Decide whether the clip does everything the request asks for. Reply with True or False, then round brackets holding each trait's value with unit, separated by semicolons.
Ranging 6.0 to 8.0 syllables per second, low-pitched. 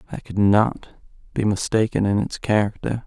False (4.9 syllables/s; 105 Hz)